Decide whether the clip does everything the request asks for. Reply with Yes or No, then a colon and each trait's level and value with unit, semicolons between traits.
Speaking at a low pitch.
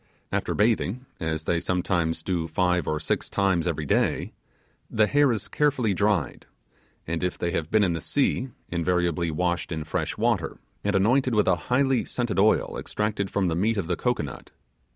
Yes: very low, 90 Hz